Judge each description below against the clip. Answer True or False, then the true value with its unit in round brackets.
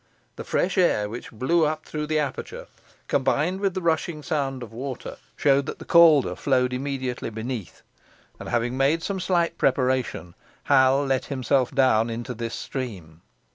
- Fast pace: False (160 wpm)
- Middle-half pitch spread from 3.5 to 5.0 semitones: True (4.0 semitones)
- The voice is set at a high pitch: False (135 Hz)